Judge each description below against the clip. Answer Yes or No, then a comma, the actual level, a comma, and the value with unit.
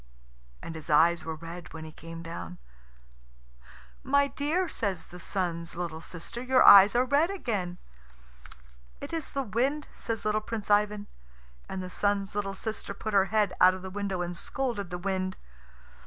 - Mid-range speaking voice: No, high, 195 Hz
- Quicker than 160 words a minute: Yes, average, 170 wpm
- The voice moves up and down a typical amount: Yes, average, 4.5 semitones